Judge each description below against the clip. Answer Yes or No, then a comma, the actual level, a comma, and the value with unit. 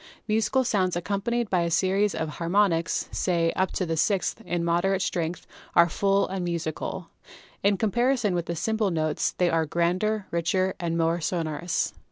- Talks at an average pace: Yes, average, 165 wpm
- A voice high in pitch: No, medium, 180 Hz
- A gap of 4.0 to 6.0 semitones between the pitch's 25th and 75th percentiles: No, average, 3.0 semitones